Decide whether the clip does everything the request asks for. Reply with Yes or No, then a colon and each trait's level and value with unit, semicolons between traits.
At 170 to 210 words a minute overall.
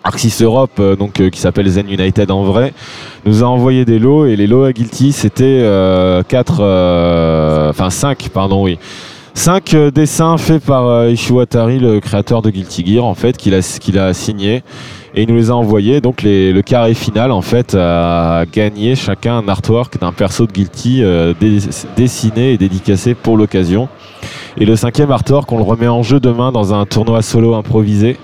Yes: average, 195 wpm